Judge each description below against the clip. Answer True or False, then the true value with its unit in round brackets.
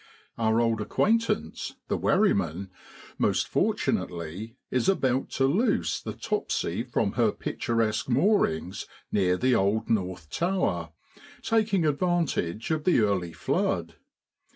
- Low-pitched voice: True (115 Hz)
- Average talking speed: False (115 wpm)